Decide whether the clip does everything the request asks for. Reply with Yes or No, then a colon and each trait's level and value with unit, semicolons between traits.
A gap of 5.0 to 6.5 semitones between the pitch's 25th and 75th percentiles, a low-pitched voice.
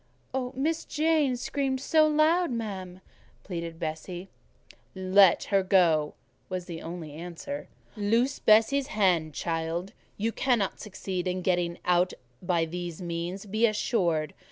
No: average, 5.3 semitones; medium, 185 Hz